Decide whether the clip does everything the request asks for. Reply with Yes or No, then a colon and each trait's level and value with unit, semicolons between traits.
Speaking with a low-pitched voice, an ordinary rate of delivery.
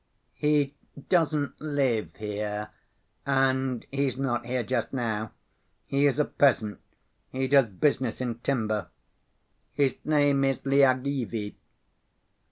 No: low, 130 Hz; slow, 110 wpm